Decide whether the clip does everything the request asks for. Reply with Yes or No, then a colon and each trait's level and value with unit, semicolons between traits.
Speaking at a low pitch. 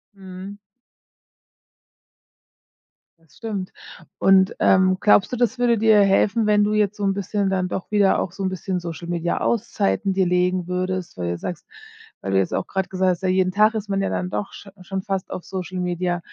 No: high, 190 Hz